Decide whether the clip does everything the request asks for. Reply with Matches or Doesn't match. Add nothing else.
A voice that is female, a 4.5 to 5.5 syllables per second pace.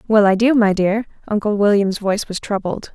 Matches